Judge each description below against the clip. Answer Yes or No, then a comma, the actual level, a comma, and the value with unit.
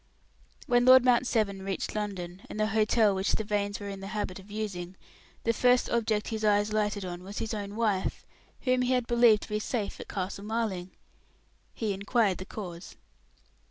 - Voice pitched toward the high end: Yes, high, 210 Hz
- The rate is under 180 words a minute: No, average, 190 wpm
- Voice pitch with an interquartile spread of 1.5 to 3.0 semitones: Yes, narrow, 2.5 semitones